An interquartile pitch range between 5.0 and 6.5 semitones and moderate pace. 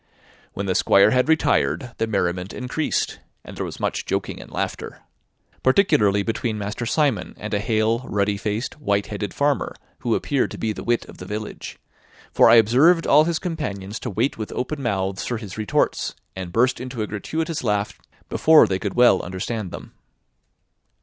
No: average, 4.1 semitones; average, 175 wpm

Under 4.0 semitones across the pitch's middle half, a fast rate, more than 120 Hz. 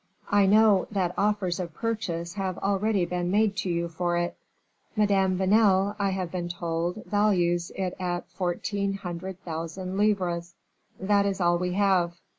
No: narrow, 2.5 semitones; average, 155 wpm; medium, 185 Hz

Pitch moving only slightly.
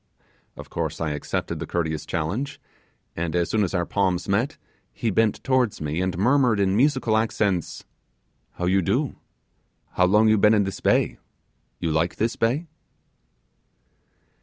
No: average, 4.4 semitones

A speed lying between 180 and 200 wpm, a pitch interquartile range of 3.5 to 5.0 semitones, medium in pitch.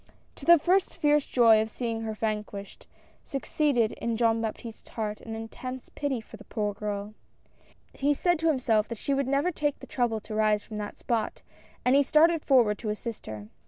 No: average, 195 wpm; average, 4.5 semitones; high, 230 Hz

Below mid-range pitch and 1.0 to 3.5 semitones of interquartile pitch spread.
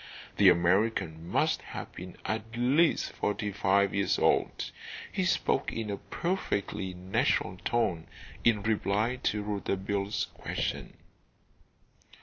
Yes: low, 100 Hz; average, 3.0 semitones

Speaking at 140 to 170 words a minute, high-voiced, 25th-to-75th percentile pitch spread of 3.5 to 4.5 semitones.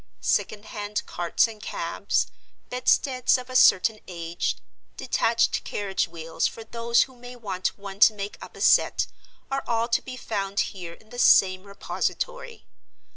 Yes: average, 155 wpm; high, 215 Hz; average, 4.0 semitones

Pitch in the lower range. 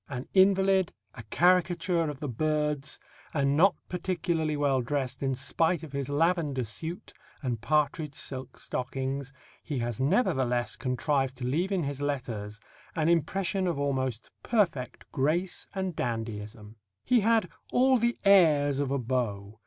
No: medium, 145 Hz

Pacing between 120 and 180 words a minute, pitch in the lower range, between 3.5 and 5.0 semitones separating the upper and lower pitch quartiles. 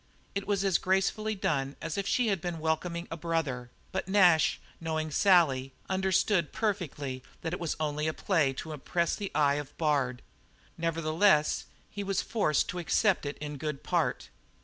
No: average, 170 wpm; medium, 165 Hz; average, 4.2 semitones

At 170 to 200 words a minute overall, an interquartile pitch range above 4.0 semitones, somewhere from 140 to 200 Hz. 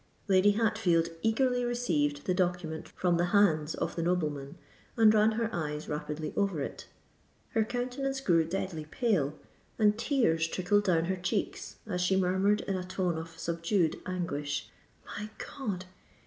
No: average, 150 wpm; average, 4.6 semitones; medium, 185 Hz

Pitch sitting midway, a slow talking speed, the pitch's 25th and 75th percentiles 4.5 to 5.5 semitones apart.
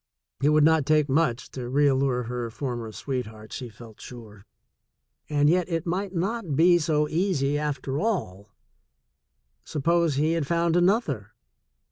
No: medium, 145 Hz; average, 145 wpm; average, 5.2 semitones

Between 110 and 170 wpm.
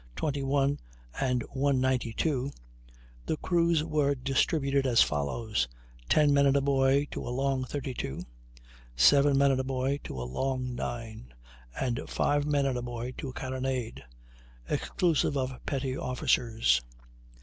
Yes: average, 140 wpm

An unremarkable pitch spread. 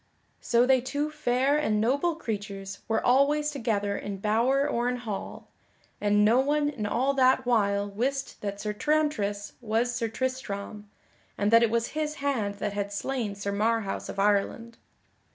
Yes: average, 4.6 semitones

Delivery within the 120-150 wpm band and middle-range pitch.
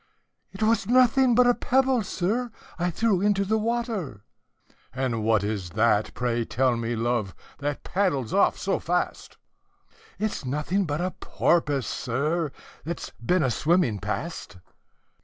Yes: average, 145 wpm; medium, 160 Hz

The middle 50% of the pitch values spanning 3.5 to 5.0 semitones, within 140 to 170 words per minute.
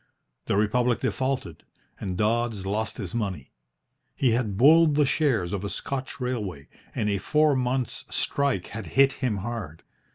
Yes: average, 4.7 semitones; average, 155 wpm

